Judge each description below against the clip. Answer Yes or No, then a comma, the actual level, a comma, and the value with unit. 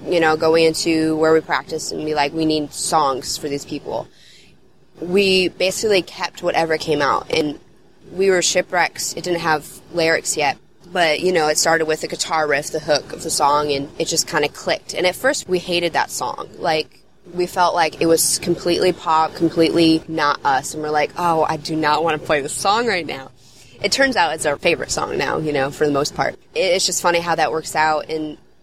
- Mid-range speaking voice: Yes, medium, 160 Hz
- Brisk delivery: Yes, fast, 220 wpm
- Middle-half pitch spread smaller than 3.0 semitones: Yes, narrow, 2.4 semitones